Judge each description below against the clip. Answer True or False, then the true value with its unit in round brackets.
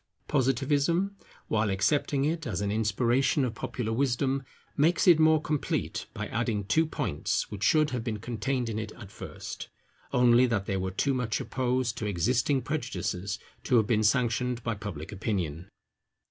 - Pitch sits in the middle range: False (120 Hz)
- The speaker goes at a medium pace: True (160 wpm)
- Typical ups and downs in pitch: True (4.6 semitones)